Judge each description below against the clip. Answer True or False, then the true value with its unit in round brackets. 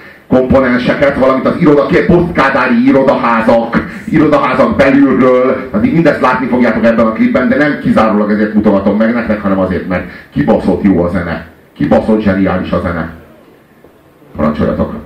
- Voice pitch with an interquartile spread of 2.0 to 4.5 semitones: False (5.0 semitones)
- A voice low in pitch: True (110 Hz)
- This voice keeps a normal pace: True (135 wpm)